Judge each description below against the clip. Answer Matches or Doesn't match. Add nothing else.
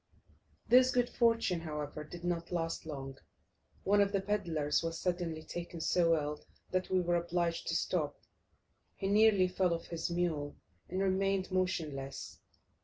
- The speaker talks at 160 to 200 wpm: Doesn't match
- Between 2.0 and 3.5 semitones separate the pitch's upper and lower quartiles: Matches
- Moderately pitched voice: Matches